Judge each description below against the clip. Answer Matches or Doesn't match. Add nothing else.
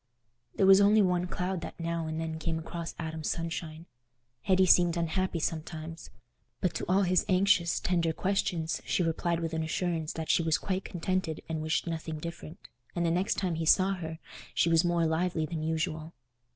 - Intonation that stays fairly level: Matches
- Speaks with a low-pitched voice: Doesn't match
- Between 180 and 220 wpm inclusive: Matches